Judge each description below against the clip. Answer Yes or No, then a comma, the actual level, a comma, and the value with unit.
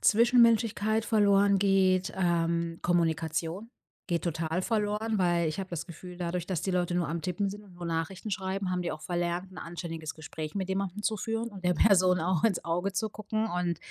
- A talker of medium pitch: Yes, medium, 180 Hz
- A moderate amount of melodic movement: Yes, average, 3.0 semitones